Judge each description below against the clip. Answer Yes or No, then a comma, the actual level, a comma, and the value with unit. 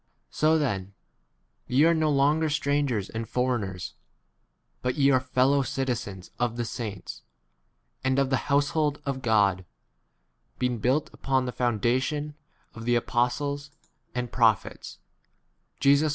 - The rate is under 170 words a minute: Yes, average, 140 wpm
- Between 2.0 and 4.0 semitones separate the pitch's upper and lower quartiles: Yes, average, 3.4 semitones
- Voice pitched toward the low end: Yes, low, 130 Hz